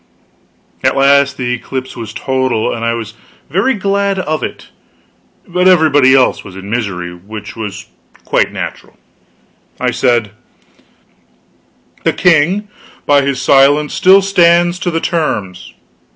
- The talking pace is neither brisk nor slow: No, slow, 130 wpm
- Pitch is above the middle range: No, medium, 140 Hz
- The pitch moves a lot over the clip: Yes, wide, 7.2 semitones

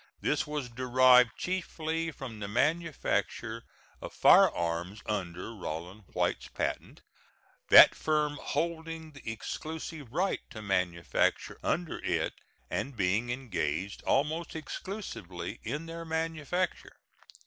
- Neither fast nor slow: No, slow, 105 wpm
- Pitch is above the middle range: No, low, 135 Hz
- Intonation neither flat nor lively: No, wide, 7.3 semitones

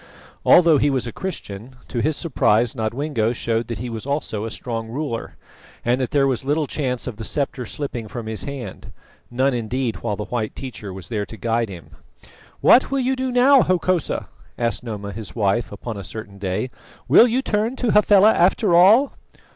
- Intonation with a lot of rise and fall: Yes, wide, 5.8 semitones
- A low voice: Yes, low, 125 Hz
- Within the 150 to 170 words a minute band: No, average, 190 wpm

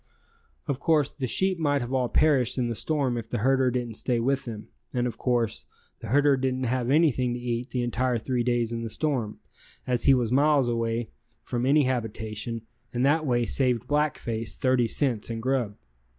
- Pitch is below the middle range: Yes, low, 125 Hz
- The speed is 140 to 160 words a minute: No, average, 195 wpm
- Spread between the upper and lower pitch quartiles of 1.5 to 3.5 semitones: Yes, narrow, 2.6 semitones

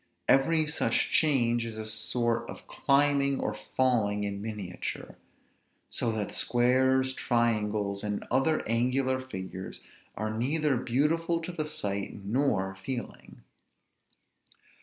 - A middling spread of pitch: Yes, average, 4.4 semitones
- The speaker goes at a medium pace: No, slow, 115 wpm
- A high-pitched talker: No, low, 120 Hz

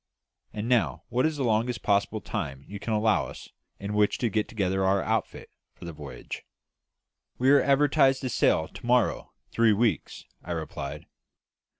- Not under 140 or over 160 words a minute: No, average, 170 wpm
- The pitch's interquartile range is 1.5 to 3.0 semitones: No, average, 4.4 semitones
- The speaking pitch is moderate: No, low, 110 Hz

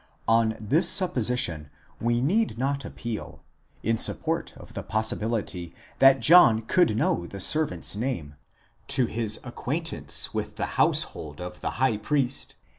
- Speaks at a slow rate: No, average, 145 wpm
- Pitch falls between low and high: No, low, 115 Hz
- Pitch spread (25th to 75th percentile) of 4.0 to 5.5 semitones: Yes, average, 4.3 semitones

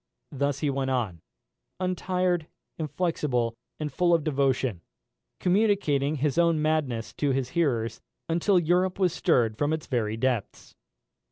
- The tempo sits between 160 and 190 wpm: No, slow, 135 wpm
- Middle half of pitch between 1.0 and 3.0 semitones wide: No, average, 4.9 semitones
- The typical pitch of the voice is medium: Yes, medium, 150 Hz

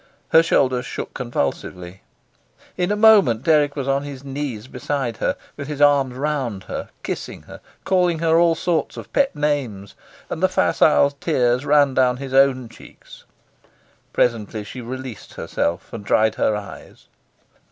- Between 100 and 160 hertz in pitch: Yes, low, 135 Hz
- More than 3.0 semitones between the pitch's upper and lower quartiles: Yes, average, 4.0 semitones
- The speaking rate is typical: Yes, average, 150 wpm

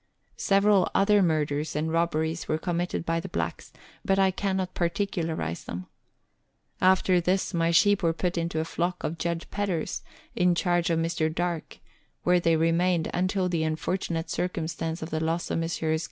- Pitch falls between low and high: Yes, medium, 170 Hz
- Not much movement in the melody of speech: Yes, narrow, 2.1 semitones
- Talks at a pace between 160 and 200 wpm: Yes, average, 170 wpm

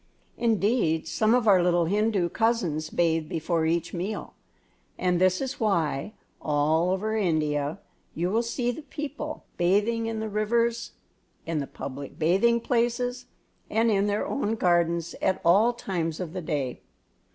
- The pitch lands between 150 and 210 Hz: Yes, high, 190 Hz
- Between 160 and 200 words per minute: No, average, 150 wpm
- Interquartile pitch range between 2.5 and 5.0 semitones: No, wide, 5.5 semitones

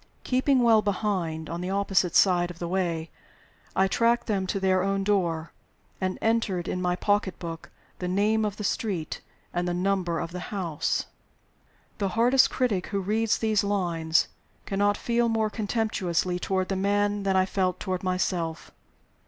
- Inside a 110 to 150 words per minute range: No, average, 160 wpm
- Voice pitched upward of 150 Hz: Yes, high, 190 Hz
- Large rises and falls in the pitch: No, average, 2.7 semitones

